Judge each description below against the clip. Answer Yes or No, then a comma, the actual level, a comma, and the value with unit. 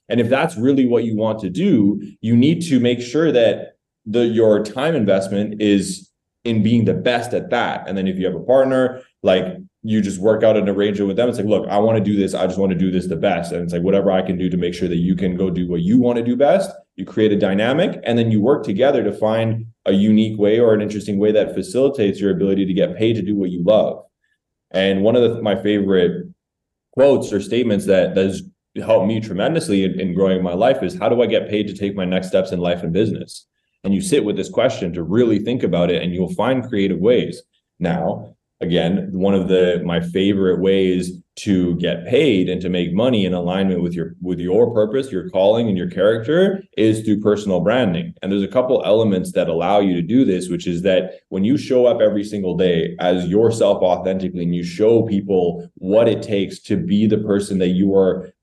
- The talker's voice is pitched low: Yes, low, 100 Hz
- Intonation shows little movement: No, average, 3.2 semitones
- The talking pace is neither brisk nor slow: No, fast, 235 wpm